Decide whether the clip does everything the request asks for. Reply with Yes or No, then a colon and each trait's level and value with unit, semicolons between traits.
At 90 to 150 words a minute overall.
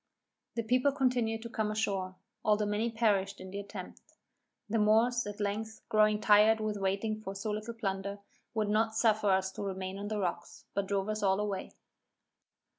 No: average, 180 wpm